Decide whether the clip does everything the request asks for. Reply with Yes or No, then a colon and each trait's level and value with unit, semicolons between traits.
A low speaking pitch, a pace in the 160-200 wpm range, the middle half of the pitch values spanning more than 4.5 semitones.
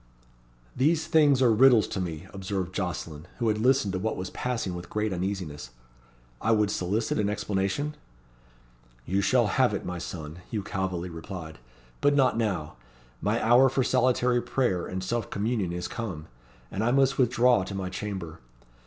Yes: low, 100 Hz; average, 170 wpm; average, 5.1 semitones